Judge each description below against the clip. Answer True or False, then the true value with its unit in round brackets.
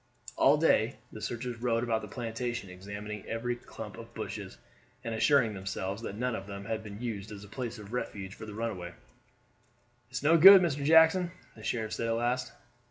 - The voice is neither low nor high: False (115 Hz)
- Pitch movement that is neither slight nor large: True (3.2 semitones)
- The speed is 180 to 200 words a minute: True (190 wpm)